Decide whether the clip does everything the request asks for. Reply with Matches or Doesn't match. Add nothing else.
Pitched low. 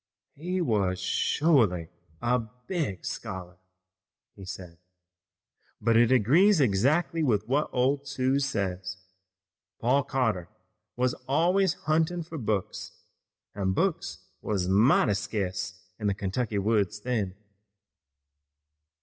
Matches